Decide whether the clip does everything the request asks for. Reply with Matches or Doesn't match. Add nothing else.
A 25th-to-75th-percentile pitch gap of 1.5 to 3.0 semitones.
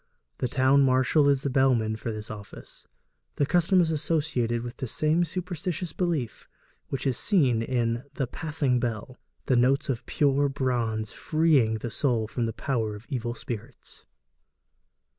Doesn't match